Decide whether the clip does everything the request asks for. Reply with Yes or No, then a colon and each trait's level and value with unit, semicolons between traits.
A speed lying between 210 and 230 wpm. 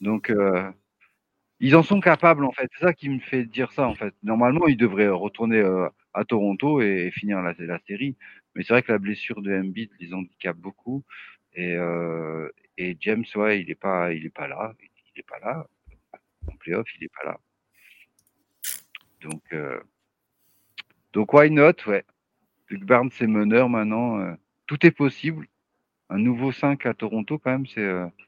No: average, 185 wpm